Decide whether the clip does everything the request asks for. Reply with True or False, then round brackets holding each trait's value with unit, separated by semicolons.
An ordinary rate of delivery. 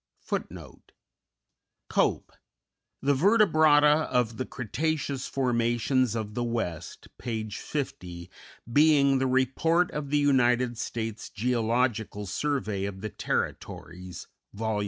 False (100 wpm)